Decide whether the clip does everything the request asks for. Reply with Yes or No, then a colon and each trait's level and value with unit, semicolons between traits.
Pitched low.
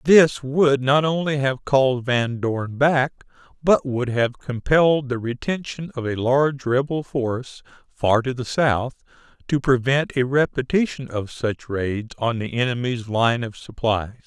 Yes: low, 130 Hz